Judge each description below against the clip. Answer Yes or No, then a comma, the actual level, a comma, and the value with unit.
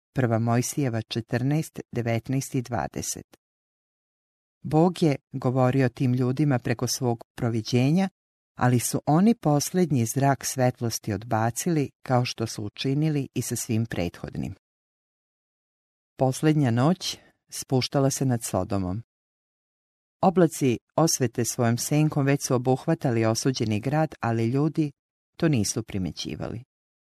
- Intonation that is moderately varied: Yes, average, 3.9 semitones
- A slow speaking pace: Yes, slow, 100 wpm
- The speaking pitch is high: No, low, 130 Hz